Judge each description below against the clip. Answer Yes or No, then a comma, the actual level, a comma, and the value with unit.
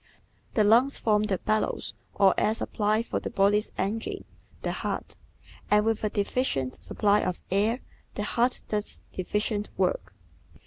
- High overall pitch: Yes, high, 210 Hz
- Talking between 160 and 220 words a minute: No, average, 145 wpm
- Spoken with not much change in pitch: Yes, narrow, 1.7 semitones